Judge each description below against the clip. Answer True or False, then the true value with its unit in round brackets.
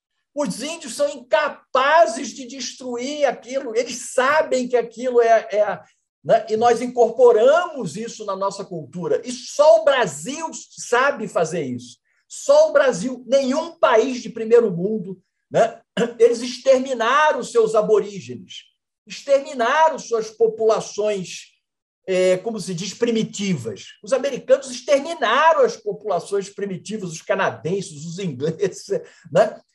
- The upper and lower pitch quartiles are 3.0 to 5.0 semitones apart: False (5.5 semitones)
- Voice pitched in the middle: False (240 Hz)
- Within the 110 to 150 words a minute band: True (125 wpm)